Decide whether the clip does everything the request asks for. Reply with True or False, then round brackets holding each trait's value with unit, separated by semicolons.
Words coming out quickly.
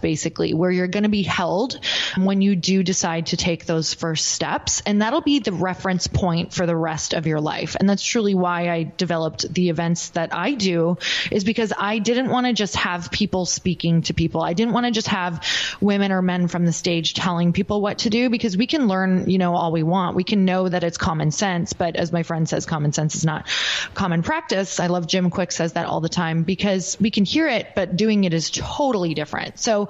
True (235 wpm)